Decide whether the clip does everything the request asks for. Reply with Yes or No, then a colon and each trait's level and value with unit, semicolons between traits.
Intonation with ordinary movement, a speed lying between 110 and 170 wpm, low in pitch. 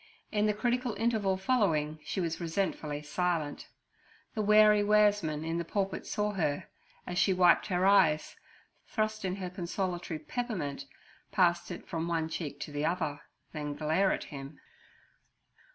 No: average, 4.8 semitones; average, 150 wpm; medium, 180 Hz